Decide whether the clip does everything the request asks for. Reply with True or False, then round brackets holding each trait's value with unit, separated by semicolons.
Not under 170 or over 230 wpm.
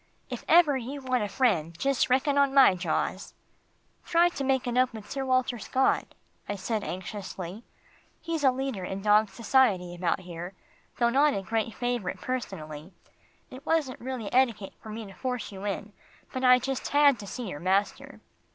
True (180 wpm)